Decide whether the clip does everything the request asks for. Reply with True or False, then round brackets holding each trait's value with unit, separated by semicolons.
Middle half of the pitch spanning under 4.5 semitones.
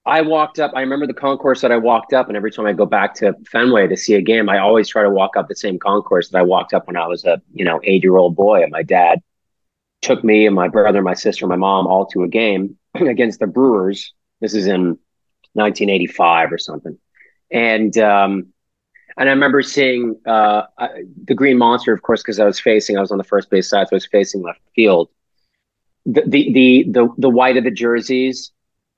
False (4.8 semitones)